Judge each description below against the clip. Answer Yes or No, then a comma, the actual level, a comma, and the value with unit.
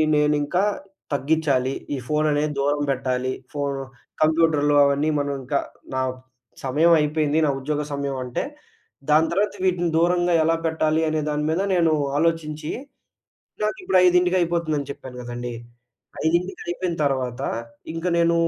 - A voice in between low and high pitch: Yes, medium, 155 Hz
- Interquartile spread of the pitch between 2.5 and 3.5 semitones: Yes, average, 3.0 semitones